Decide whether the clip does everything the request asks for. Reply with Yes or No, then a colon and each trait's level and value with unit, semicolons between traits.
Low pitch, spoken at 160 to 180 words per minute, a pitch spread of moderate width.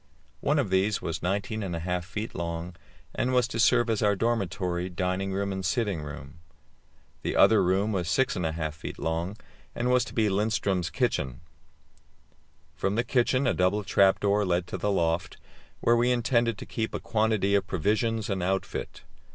Yes: low, 100 Hz; average, 175 wpm; average, 4.0 semitones